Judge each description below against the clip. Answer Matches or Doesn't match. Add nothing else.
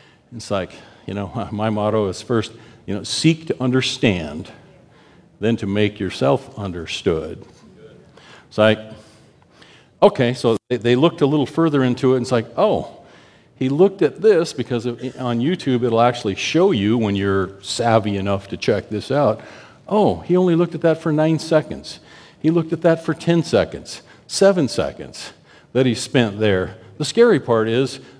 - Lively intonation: Matches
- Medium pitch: Doesn't match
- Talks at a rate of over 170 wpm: Doesn't match